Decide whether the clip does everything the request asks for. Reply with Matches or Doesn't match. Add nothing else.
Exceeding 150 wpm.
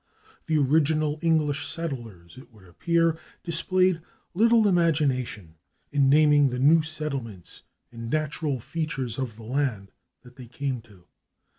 Doesn't match